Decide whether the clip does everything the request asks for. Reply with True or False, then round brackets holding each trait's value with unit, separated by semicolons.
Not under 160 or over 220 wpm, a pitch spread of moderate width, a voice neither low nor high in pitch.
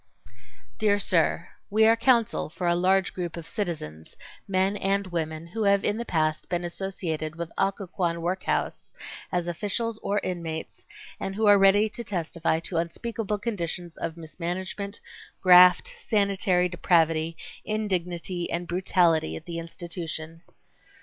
False (135 wpm; 3.0 semitones; 180 Hz)